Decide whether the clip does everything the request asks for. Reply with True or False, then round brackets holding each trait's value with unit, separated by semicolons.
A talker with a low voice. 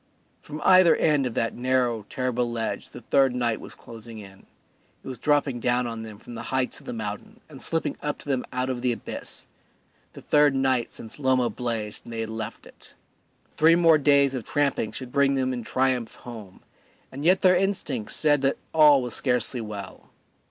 True (125 Hz)